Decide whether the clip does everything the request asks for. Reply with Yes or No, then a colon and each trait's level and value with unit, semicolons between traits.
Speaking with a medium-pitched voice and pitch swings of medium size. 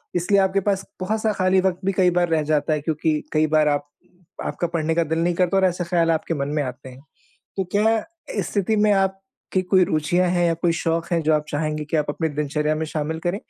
Yes: medium, 170 Hz; average, 3.5 semitones